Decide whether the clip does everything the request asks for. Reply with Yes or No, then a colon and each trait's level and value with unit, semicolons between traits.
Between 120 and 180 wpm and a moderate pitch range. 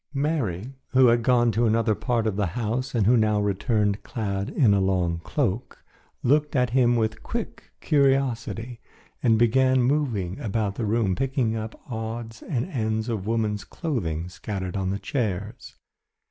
Yes: average, 160 wpm; average, 3.4 semitones